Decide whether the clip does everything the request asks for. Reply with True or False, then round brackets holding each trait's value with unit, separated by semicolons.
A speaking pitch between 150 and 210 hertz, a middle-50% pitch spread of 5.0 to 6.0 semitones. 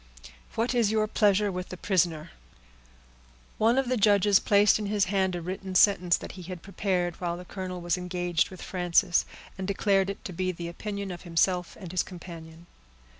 False (185 Hz; 2.4 semitones)